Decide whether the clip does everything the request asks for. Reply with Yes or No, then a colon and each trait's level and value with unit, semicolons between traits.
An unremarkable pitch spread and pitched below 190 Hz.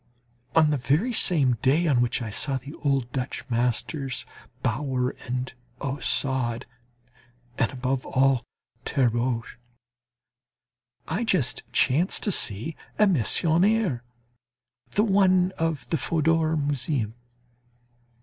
Yes: average, 4.7 semitones; low, 135 Hz